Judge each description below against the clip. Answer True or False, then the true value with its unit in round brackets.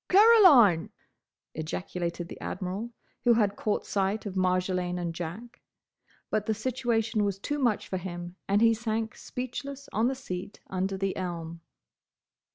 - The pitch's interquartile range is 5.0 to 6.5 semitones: False (4.5 semitones)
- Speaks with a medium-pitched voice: False (200 Hz)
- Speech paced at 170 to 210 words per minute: False (145 wpm)